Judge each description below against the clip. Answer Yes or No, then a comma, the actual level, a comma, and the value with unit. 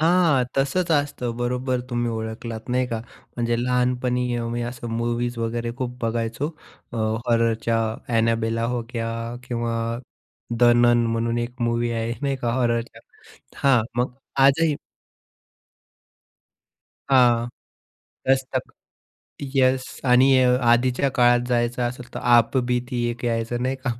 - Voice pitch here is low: Yes, low, 120 Hz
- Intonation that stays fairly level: Yes, narrow, 1.4 semitones